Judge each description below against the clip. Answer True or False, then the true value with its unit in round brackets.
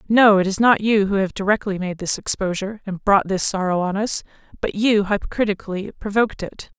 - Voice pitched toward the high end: True (200 Hz)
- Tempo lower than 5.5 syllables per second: False (5.8 syllables/s)